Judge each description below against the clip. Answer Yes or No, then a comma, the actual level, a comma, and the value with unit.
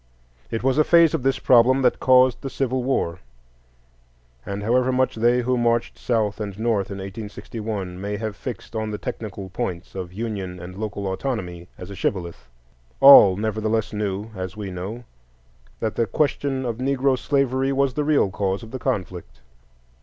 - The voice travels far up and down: No, average, 4.7 semitones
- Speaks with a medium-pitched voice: No, low, 110 Hz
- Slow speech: No, average, 170 wpm